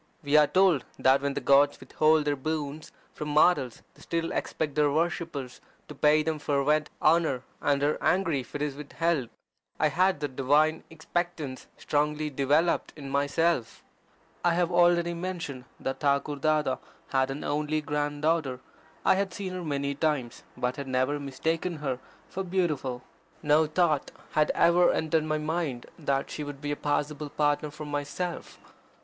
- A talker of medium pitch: Yes, medium, 150 Hz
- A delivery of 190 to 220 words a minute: No, average, 165 wpm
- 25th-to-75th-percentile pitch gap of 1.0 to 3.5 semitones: Yes, narrow, 2.6 semitones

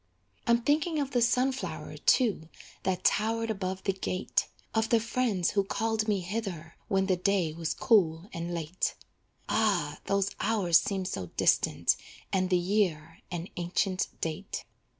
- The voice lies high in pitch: Yes, high, 195 Hz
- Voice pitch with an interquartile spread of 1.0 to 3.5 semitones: No, average, 4.2 semitones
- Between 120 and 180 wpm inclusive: Yes, average, 150 wpm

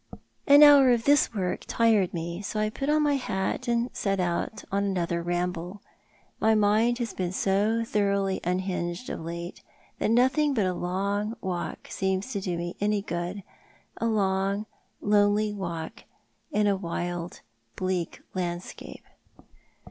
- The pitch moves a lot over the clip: No, average, 3.7 semitones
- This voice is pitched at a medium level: No, high, 195 Hz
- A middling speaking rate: Yes, average, 150 wpm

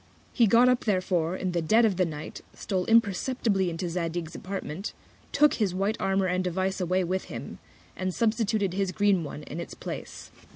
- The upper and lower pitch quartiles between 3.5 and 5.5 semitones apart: No, average, 2.9 semitones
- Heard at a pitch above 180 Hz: Yes, high, 190 Hz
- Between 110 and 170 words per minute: No, average, 180 wpm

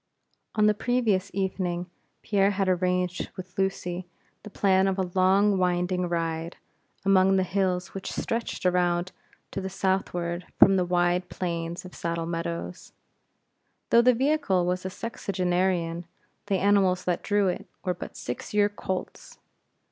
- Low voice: No, medium, 185 Hz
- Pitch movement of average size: No, narrow, 1.7 semitones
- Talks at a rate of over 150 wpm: No, average, 145 wpm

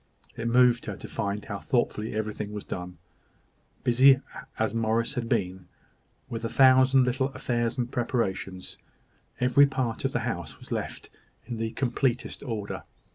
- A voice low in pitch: Yes, low, 120 Hz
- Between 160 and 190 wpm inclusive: No, average, 150 wpm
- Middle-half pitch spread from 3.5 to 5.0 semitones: No, average, 2.9 semitones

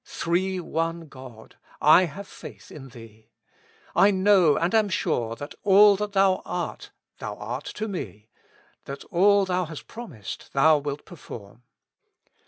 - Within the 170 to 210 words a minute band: No, average, 145 wpm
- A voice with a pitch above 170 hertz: No, medium, 165 Hz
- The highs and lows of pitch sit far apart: Yes, wide, 6.5 semitones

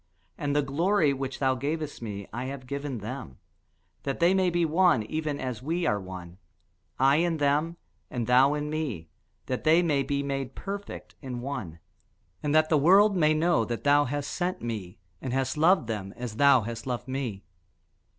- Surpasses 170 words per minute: Yes, average, 185 wpm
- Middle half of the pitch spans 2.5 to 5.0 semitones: Yes, average, 4.4 semitones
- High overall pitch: No, medium, 140 Hz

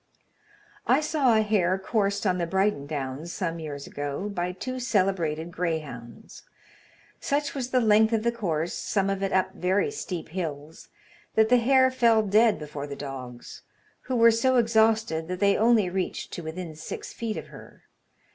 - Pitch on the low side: No, high, 190 Hz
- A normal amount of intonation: No, wide, 5.8 semitones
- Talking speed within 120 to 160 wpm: No, average, 170 wpm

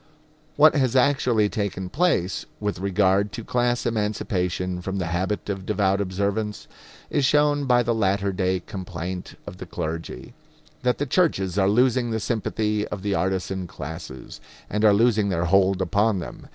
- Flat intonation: No, average, 3.6 semitones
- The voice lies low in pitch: Yes, low, 100 Hz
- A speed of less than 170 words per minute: Yes, average, 160 wpm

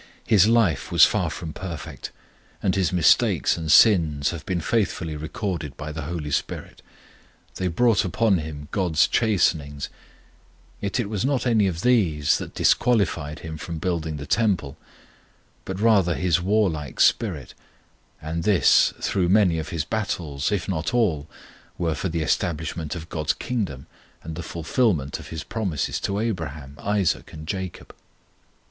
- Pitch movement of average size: Yes, average, 4.6 semitones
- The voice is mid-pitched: No, very low, 85 Hz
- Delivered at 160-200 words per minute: No, average, 150 wpm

